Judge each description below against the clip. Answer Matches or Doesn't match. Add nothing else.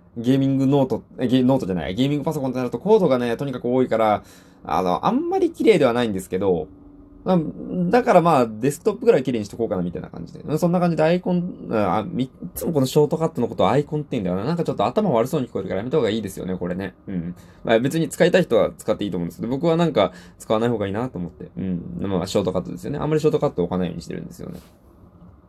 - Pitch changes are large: Matches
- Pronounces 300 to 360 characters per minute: Doesn't match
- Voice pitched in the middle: Doesn't match